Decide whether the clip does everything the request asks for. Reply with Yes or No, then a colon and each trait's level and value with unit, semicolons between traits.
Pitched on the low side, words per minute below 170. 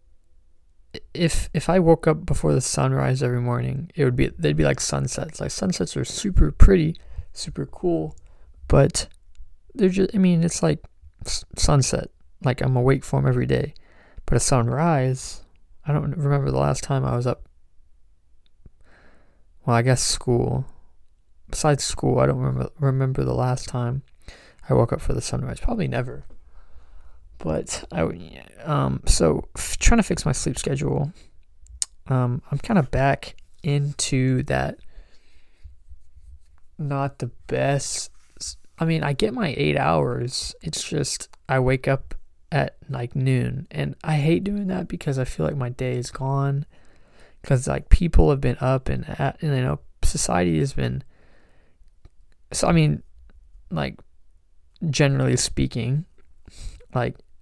Yes: very low, 90 Hz; average, 145 wpm